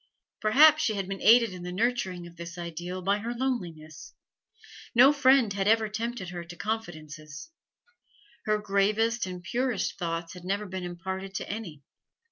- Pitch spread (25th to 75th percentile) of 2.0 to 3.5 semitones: No, average, 4.4 semitones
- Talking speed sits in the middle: Yes, average, 160 wpm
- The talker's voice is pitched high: Yes, high, 195 Hz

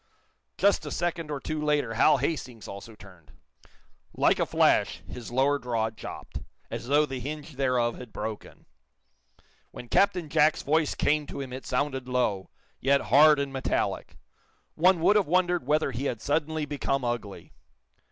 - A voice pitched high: No, medium, 140 Hz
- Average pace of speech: Yes, average, 160 wpm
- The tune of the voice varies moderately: Yes, average, 3.9 semitones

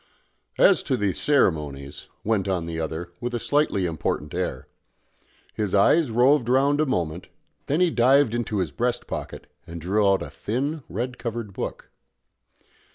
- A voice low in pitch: Yes, low, 105 Hz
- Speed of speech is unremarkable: Yes, average, 160 wpm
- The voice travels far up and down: Yes, wide, 6.8 semitones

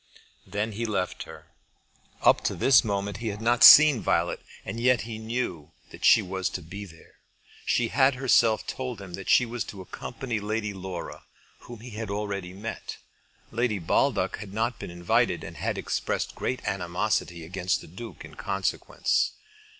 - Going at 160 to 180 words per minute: Yes, average, 170 wpm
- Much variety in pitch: No, average, 3.8 semitones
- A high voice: No, low, 105 Hz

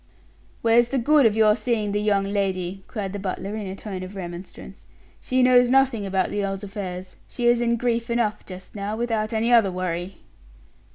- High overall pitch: Yes, high, 210 Hz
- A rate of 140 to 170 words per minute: No, average, 190 wpm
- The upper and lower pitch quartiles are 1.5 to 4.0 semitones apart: Yes, average, 3.4 semitones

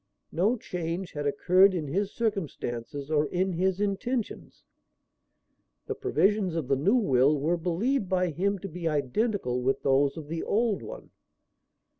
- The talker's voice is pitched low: No, medium, 180 Hz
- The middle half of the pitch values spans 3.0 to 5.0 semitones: No, wide, 5.6 semitones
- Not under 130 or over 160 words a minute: Yes, average, 150 wpm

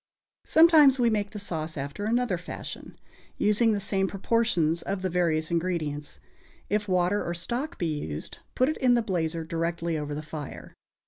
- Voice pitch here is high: No, medium, 180 Hz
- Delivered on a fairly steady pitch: No, average, 5.1 semitones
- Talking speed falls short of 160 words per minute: No, average, 170 wpm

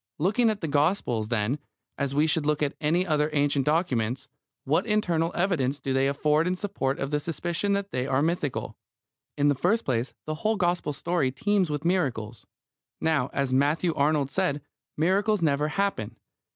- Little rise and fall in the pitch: No, average, 4.4 semitones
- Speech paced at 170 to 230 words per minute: Yes, average, 175 wpm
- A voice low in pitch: No, medium, 150 Hz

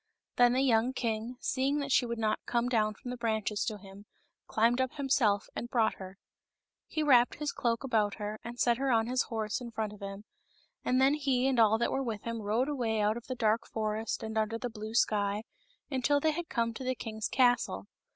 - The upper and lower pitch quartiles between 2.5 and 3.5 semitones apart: Yes, average, 2.9 semitones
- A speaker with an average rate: No, fast, 220 wpm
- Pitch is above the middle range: Yes, high, 230 Hz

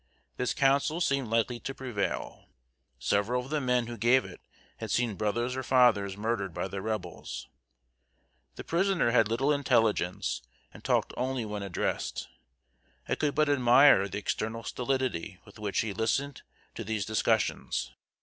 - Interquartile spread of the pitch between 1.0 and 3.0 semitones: No, average, 4.1 semitones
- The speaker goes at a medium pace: Yes, average, 150 wpm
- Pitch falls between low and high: No, low, 120 Hz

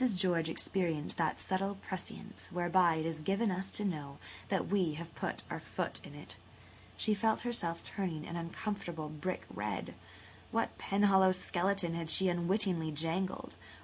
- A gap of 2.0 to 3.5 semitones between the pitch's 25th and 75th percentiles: Yes, average, 2.9 semitones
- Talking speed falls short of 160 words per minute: Yes, average, 150 wpm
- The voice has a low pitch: No, medium, 180 Hz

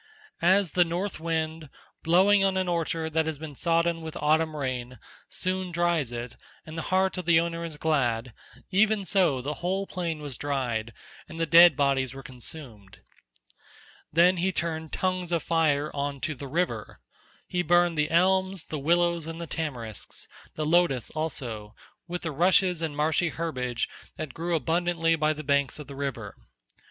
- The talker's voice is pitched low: No, medium, 160 Hz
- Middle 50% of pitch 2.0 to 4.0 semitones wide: Yes, average, 3.5 semitones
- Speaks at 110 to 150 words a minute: No, average, 165 wpm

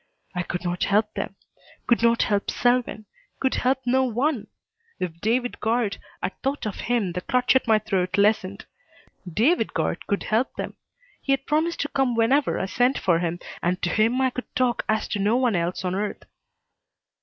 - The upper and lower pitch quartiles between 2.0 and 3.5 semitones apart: No, average, 4.4 semitones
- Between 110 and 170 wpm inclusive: No, average, 190 wpm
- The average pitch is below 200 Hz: No, high, 225 Hz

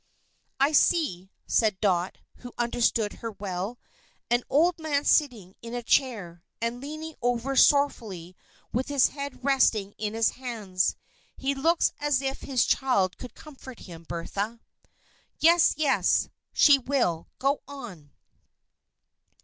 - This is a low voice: No, high, 245 Hz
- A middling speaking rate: No, slow, 130 wpm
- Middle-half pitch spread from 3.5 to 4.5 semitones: No, wide, 5.6 semitones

